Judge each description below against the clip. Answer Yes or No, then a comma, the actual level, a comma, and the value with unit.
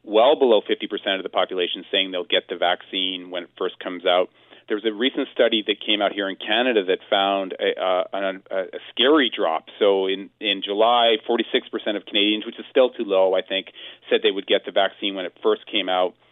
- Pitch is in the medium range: No, low, 100 Hz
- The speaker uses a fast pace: Yes, fast, 230 wpm